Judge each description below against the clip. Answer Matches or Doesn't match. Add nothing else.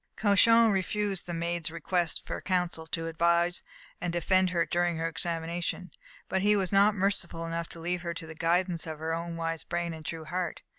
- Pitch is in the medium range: Matches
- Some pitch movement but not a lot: Doesn't match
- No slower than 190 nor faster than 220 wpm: Matches